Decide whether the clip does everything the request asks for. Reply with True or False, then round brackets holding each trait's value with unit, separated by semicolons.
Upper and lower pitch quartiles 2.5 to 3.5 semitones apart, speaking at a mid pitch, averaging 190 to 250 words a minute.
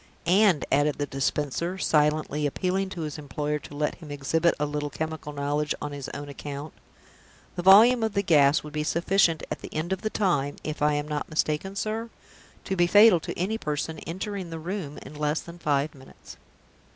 False (3.9 semitones; 155 Hz; 195 wpm)